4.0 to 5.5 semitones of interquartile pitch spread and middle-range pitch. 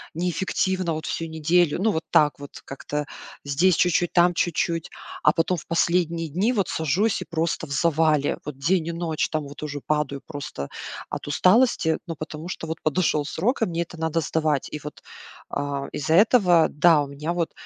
No: average, 2.9 semitones; medium, 160 Hz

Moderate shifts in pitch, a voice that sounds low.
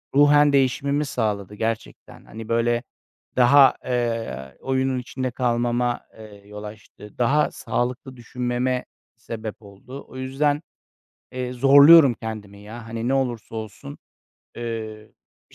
Yes: average, 3.1 semitones; low, 120 Hz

